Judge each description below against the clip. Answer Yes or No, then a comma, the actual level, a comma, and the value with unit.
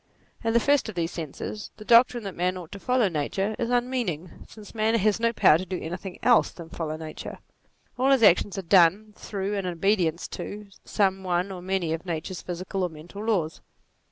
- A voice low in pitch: No, high, 190 Hz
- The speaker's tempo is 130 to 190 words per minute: No, fast, 205 wpm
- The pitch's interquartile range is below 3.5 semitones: No, average, 4.0 semitones